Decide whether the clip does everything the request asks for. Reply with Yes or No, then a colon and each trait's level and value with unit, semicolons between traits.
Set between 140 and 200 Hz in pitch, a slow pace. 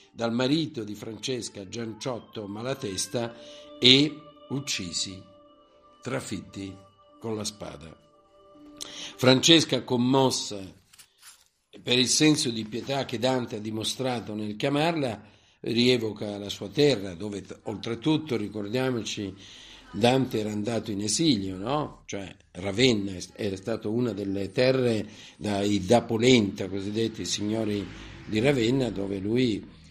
No: low, 115 Hz; slow, 110 wpm